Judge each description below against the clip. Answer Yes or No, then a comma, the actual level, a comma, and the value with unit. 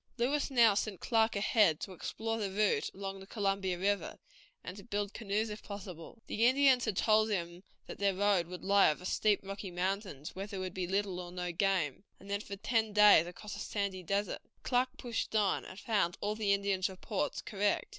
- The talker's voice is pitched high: Yes, high, 200 Hz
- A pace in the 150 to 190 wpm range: No, average, 200 wpm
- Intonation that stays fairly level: Yes, narrow, 2.3 semitones